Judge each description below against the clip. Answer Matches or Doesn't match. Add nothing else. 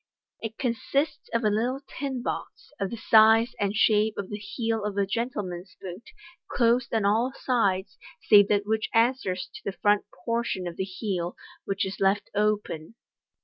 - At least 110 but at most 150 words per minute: Doesn't match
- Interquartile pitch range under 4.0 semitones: Matches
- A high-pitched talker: Matches